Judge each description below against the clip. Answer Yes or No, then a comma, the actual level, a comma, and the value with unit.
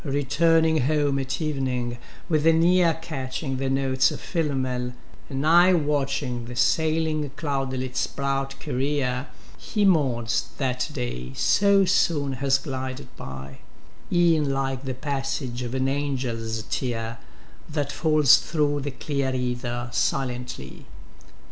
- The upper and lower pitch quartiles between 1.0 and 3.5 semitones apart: Yes, average, 3.2 semitones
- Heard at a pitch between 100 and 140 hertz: Yes, low, 135 Hz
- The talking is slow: Yes, slow, 125 wpm